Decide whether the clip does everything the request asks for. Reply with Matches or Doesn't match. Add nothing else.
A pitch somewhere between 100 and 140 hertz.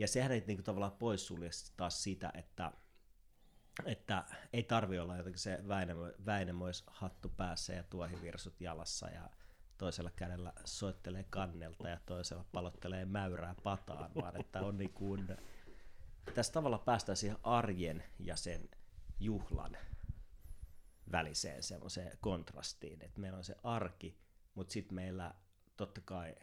Doesn't match